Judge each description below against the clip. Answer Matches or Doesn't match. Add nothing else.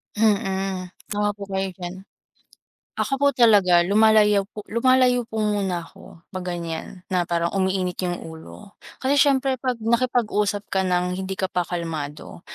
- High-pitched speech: Matches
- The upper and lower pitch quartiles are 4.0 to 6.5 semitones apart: Doesn't match